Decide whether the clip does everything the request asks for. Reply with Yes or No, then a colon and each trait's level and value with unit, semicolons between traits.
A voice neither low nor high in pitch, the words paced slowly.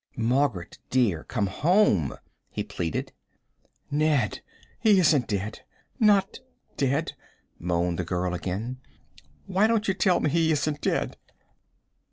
No: low, 130 Hz; slow, 120 wpm